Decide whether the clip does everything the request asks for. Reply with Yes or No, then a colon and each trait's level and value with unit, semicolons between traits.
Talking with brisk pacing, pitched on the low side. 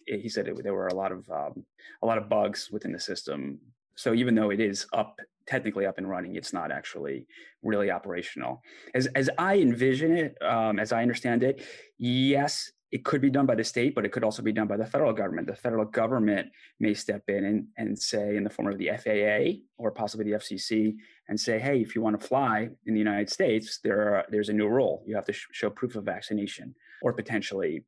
Yes: fast, 230 wpm; low, 110 Hz